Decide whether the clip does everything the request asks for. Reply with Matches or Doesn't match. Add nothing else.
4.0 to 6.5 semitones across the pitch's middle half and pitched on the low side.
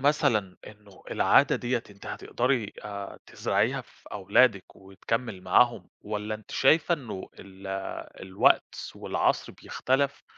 Matches